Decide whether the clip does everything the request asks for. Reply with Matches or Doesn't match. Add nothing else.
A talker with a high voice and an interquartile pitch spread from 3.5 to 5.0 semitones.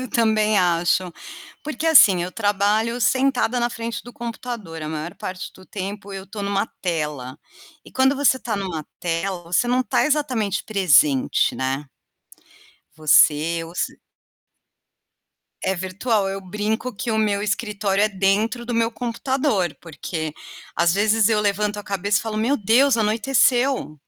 Matches